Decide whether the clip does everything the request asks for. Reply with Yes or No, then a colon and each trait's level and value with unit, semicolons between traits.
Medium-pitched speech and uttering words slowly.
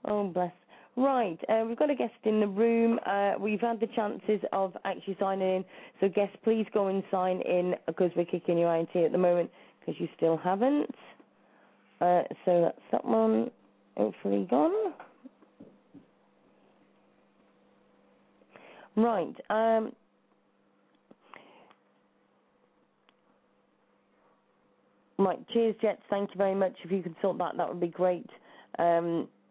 No: high, 195 Hz; slow, 130 wpm